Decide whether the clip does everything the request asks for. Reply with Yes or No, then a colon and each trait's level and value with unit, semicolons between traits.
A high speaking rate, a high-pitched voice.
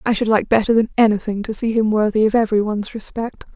Yes: fast, 235 wpm; high, 215 Hz